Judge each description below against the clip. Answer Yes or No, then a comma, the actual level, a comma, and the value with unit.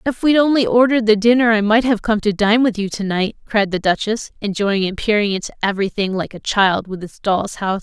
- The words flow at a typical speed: No, fast, 240 wpm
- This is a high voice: Yes, high, 210 Hz